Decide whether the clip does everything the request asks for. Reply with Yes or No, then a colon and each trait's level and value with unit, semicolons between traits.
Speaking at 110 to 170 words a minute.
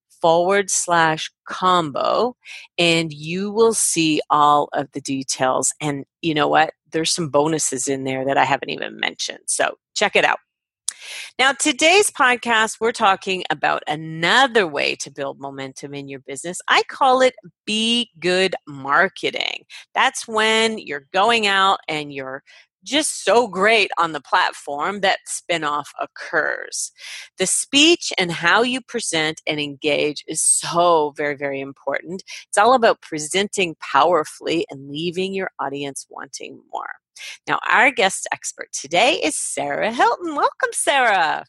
Yes: average, 145 wpm